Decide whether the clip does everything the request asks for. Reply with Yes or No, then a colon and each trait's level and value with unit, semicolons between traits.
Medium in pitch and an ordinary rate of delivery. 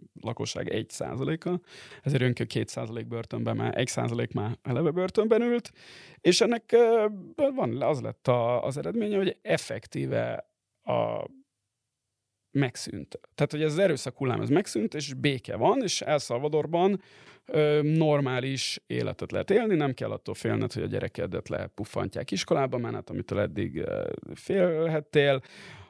Yes: medium, 150 Hz; average, 135 wpm